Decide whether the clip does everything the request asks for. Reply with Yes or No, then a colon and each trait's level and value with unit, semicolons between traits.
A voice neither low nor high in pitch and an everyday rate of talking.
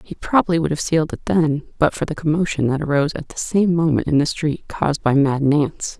No: medium, 155 Hz; fast, 240 wpm